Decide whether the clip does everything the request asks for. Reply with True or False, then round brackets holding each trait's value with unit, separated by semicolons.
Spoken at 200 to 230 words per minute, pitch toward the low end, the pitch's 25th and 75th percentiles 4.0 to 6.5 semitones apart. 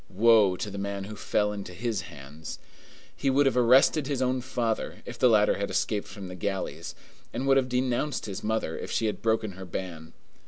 True (205 wpm; 110 Hz; 4.5 semitones)